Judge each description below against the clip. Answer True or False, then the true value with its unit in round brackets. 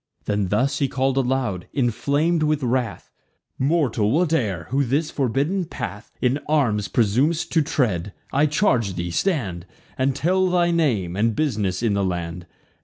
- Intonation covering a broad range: True (6.7 semitones)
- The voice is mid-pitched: False (130 Hz)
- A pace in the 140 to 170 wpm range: True (150 wpm)